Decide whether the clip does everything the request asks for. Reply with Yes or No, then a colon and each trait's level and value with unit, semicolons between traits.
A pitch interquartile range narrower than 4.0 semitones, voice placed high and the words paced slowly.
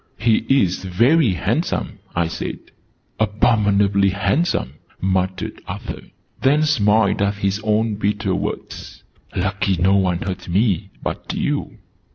No: average, 2.8 semitones; low, 100 Hz; slow, 120 wpm